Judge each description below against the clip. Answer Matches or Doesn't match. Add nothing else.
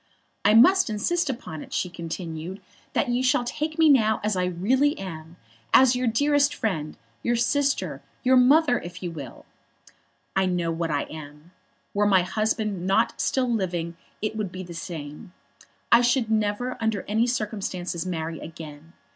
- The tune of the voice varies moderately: Doesn't match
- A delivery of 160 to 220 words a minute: Matches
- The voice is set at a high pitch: Matches